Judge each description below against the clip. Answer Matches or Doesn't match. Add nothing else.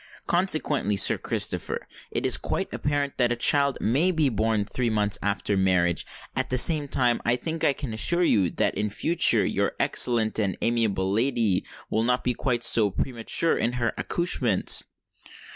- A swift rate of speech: Doesn't match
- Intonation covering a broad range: Doesn't match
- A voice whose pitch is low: Matches